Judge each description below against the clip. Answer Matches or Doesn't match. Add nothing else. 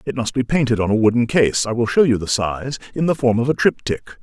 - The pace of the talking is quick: Matches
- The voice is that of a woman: Doesn't match